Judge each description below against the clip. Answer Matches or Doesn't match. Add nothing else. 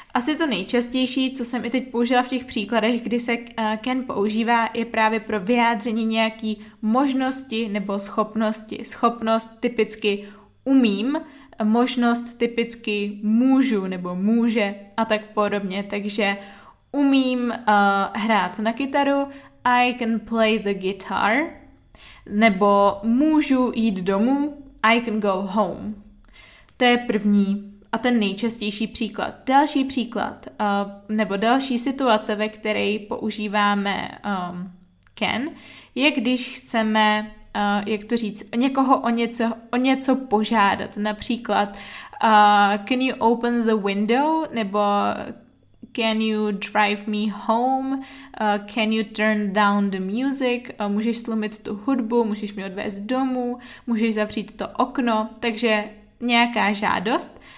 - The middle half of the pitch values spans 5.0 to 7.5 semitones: Doesn't match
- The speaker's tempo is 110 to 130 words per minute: Matches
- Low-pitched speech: Doesn't match